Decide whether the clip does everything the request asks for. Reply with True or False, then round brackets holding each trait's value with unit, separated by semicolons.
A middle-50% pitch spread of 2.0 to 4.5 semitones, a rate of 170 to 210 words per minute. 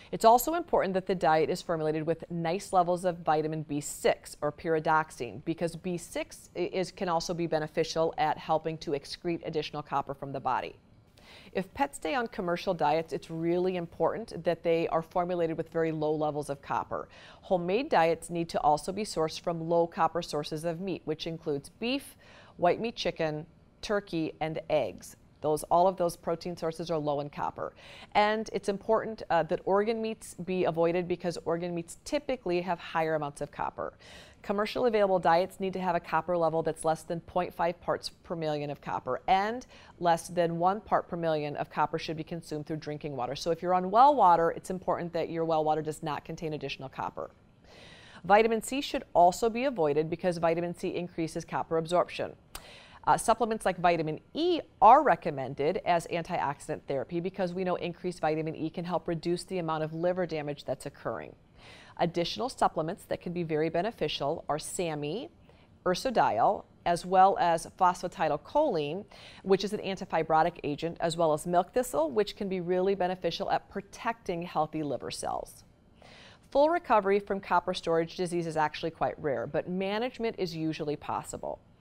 True (2.9 semitones; 175 wpm)